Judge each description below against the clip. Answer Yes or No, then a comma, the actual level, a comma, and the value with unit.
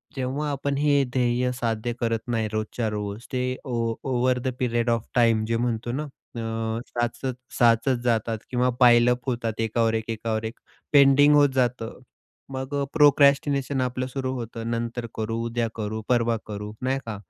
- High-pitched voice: No, low, 120 Hz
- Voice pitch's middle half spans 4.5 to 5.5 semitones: No, narrow, 2.4 semitones